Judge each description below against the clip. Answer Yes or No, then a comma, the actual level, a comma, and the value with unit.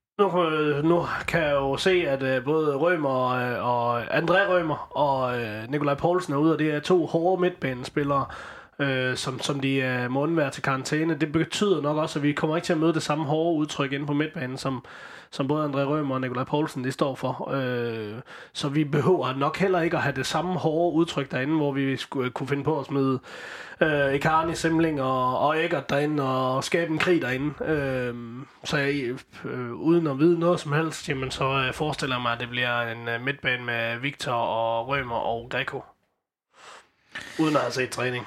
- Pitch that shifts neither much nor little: Yes, average, 3.6 semitones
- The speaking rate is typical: Yes, average, 200 wpm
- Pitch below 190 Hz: Yes, medium, 140 Hz